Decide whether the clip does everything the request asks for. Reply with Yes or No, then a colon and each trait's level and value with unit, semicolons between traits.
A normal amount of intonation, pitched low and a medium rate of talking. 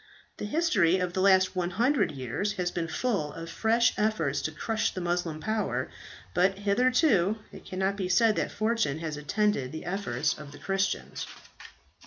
No: average, 4.9 semitones; high, 190 Hz; average, 165 wpm